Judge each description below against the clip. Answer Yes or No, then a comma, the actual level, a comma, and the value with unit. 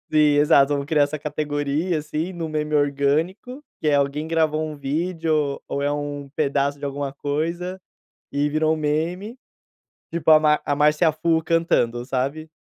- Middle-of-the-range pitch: Yes, medium, 150 Hz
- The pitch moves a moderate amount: No, narrow, 2.1 semitones